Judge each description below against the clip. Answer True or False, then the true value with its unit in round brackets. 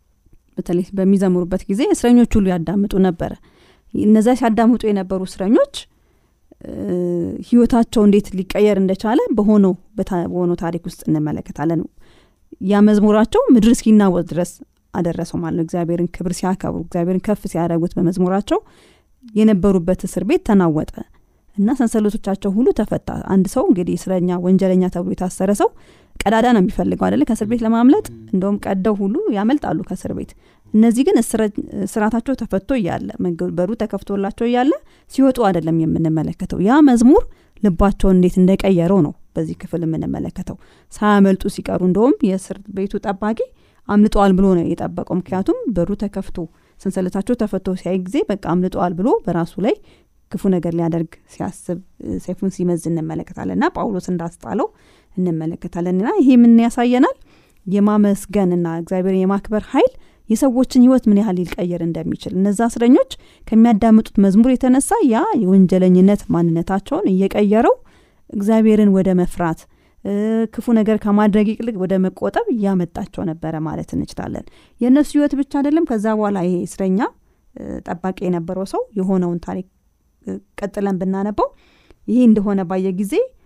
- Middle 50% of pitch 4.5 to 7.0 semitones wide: False (3.7 semitones)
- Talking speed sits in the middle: False (120 wpm)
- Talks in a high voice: True (195 Hz)